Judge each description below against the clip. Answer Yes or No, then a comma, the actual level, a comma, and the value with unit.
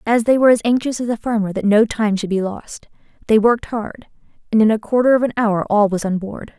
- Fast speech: Yes, fast, 255 wpm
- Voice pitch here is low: No, high, 220 Hz